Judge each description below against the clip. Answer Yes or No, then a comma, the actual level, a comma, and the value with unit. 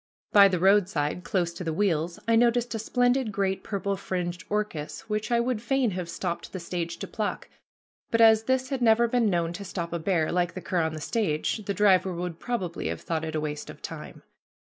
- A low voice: No, high, 190 Hz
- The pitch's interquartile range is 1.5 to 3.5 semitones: No, average, 4.6 semitones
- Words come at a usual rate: No, fast, 215 wpm